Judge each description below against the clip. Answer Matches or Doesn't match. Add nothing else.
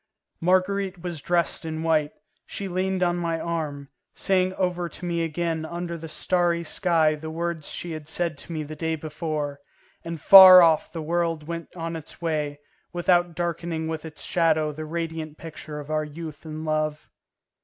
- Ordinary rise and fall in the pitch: Doesn't match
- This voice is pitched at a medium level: Matches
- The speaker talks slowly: Doesn't match